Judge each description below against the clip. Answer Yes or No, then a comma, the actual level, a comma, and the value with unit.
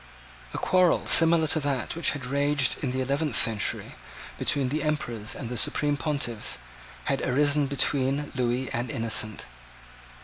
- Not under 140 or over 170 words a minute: Yes, average, 145 wpm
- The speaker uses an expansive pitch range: No, average, 3.0 semitones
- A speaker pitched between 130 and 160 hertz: Yes, medium, 140 Hz